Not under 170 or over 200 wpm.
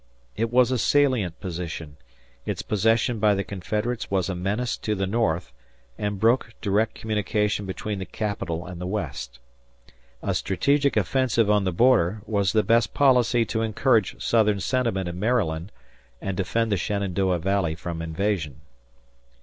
No: average, 150 wpm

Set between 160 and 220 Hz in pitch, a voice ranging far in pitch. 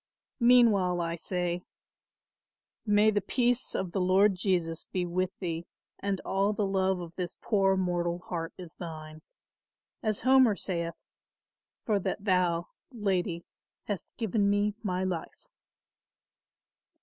No: medium, 185 Hz; average, 2.9 semitones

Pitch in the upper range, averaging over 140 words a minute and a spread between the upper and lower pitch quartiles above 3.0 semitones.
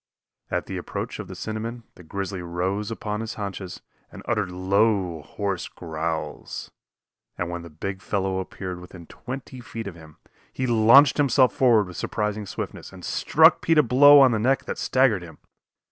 No: low, 100 Hz; average, 175 wpm; average, 4.6 semitones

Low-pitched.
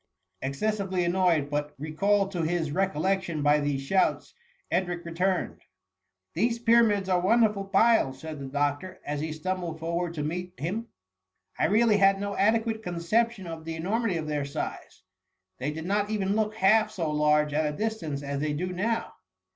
No: medium, 175 Hz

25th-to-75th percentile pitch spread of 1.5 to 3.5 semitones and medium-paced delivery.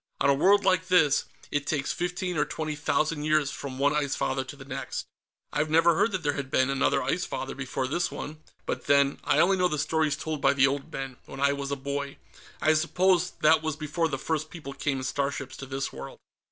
No: narrow, 2.6 semitones; fast, 230 wpm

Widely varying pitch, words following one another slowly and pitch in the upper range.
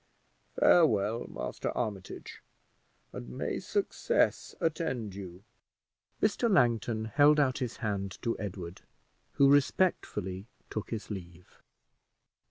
No: wide, 6.3 semitones; slow, 100 wpm; low, 110 Hz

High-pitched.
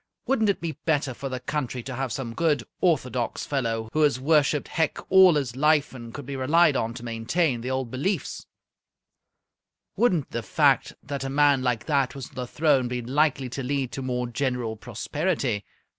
No: low, 135 Hz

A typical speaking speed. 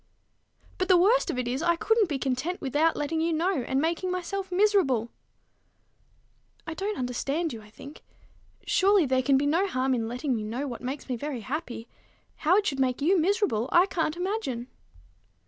Yes: average, 185 wpm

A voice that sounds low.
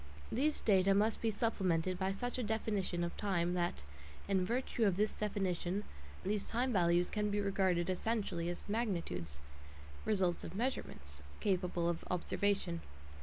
No: high, 195 Hz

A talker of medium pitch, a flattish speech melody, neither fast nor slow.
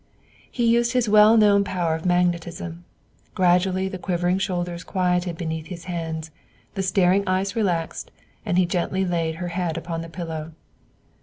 Yes: medium, 180 Hz; narrow, 2.1 semitones; average, 155 wpm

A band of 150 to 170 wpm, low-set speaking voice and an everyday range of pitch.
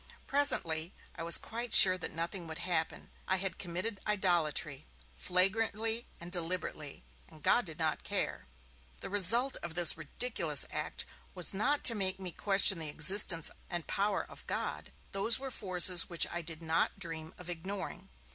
No: average, 160 wpm; medium, 180 Hz; average, 3.5 semitones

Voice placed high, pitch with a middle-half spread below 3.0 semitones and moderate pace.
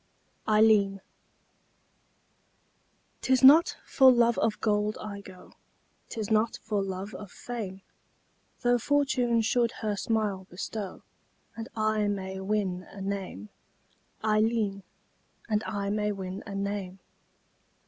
No: high, 210 Hz; narrow, 2.4 semitones; slow, 115 wpm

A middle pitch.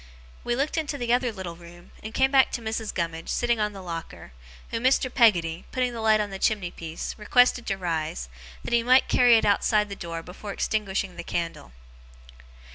No: high, 210 Hz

